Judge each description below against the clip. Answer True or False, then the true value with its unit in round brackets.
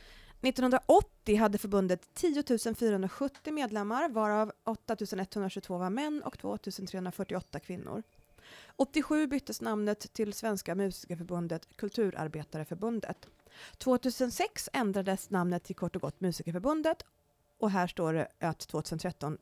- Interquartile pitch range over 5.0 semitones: True (5.5 semitones)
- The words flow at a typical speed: False (110 wpm)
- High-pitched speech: True (205 Hz)